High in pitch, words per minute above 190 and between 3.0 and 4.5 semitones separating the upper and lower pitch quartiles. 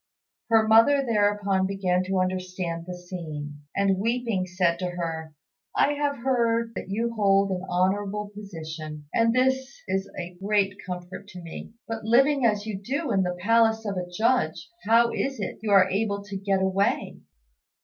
No: high, 200 Hz; average, 170 wpm; average, 3.8 semitones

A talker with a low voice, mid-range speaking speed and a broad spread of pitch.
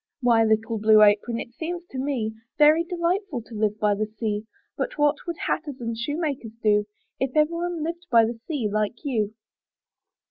No: high, 240 Hz; average, 180 wpm; wide, 6.0 semitones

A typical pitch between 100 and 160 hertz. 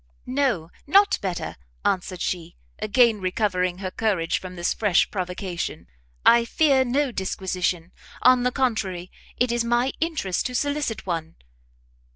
No: high, 205 Hz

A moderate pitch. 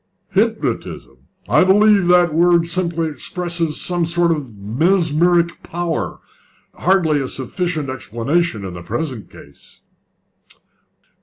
Yes: medium, 170 Hz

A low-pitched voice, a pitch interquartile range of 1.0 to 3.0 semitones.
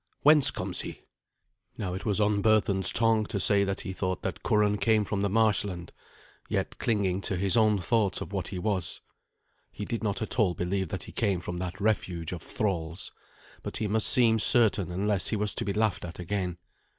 Yes: low, 100 Hz; average, 2.7 semitones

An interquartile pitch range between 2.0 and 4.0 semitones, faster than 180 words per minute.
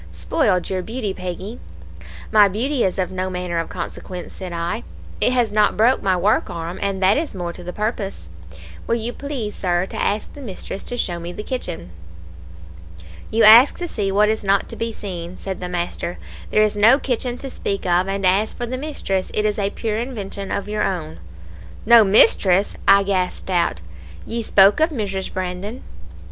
Yes: average, 3.5 semitones; average, 190 wpm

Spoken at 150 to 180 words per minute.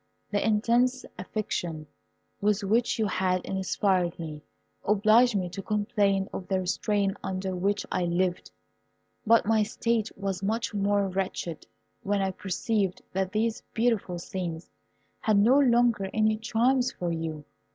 No: average, 140 wpm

